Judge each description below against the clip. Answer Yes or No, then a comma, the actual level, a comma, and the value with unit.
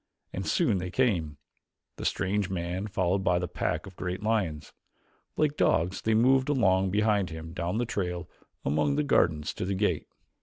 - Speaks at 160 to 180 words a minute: Yes, average, 175 wpm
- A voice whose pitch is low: Yes, very low, 95 Hz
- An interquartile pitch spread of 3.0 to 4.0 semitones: Yes, average, 3.4 semitones